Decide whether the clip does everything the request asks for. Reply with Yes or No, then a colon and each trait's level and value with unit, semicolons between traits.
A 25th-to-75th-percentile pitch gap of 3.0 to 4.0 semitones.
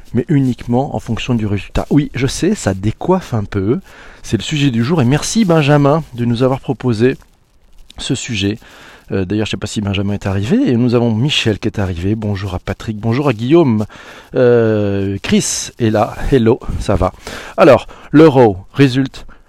No: average, 4.8 semitones